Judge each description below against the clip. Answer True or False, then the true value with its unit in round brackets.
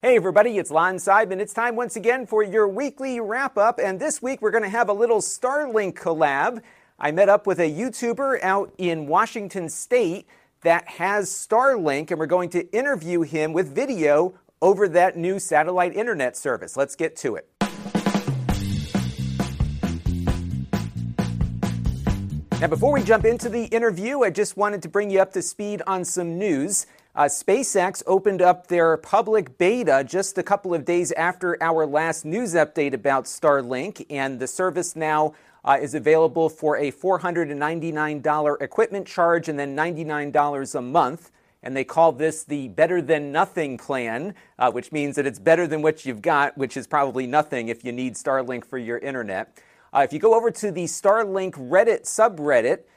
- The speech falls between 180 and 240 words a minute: False (170 wpm)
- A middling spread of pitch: False (6.0 semitones)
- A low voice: False (170 Hz)